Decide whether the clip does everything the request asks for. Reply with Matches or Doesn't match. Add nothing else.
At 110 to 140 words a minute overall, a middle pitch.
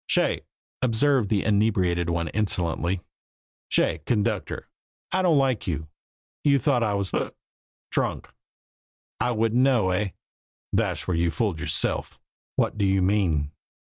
Doesn't match